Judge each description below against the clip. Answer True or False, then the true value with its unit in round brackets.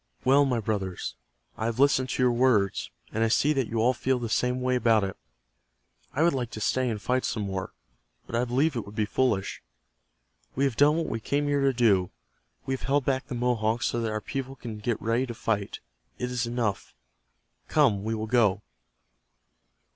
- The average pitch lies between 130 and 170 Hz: False (120 Hz)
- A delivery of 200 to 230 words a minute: True (205 wpm)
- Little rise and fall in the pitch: False (3.2 semitones)